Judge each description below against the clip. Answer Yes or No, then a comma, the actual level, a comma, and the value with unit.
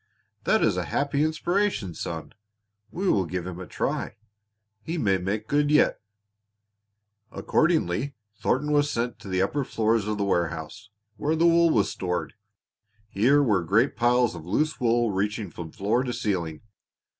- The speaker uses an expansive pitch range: Yes, wide, 7.5 semitones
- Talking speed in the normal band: Yes, average, 155 wpm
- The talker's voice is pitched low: Yes, low, 110 Hz